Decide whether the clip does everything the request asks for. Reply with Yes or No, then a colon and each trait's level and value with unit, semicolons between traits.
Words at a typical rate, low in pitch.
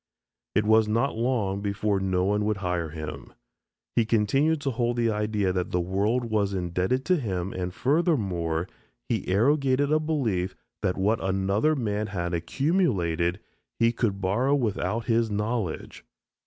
Yes: average, 150 wpm; low, 105 Hz